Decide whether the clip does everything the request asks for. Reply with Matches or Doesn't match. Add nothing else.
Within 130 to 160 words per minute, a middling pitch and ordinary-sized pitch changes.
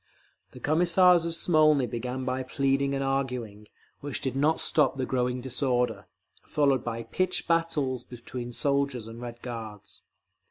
Doesn't match